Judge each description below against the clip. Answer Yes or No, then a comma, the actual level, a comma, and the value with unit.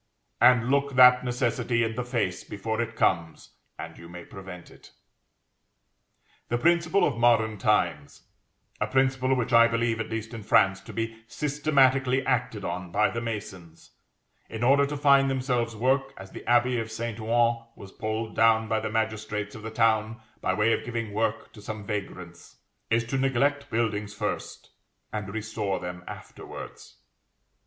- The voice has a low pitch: Yes, low, 115 Hz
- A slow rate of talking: No, average, 165 wpm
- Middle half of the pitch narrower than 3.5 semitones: Yes, average, 3.0 semitones